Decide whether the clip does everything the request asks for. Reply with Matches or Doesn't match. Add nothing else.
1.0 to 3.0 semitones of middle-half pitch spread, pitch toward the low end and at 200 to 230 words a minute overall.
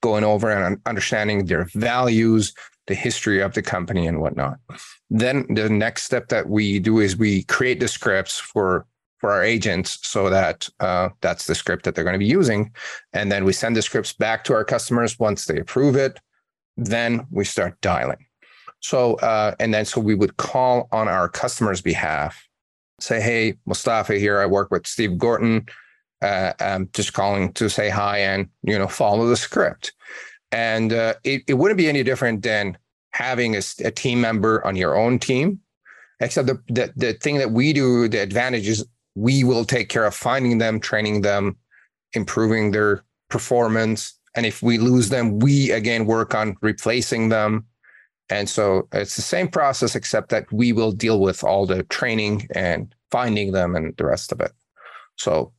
Doesn't match